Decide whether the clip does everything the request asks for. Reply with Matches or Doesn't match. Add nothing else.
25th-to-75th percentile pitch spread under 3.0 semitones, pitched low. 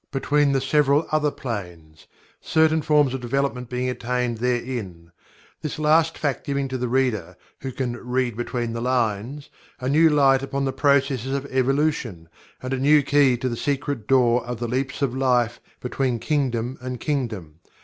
Matches